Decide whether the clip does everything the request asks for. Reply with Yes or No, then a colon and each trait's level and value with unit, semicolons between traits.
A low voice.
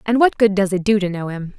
No: high, 200 Hz